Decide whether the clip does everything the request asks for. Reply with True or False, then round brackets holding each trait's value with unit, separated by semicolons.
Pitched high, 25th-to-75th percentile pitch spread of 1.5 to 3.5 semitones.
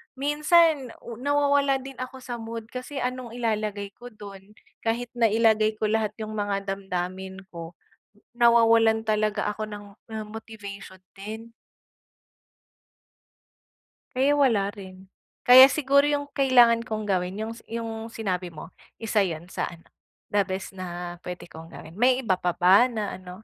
False (220 Hz; 4.0 semitones)